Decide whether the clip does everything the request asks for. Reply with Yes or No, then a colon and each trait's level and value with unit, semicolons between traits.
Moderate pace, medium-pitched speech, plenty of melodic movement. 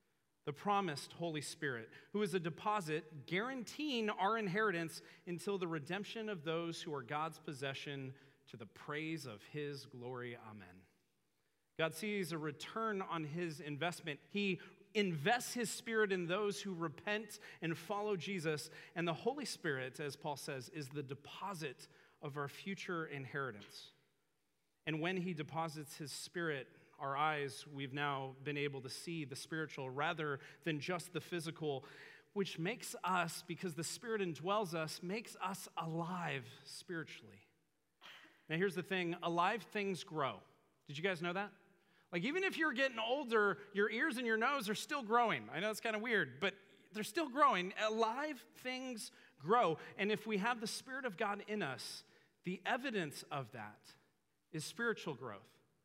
Yes: average, 160 wpm; medium, 170 Hz; wide, 5.7 semitones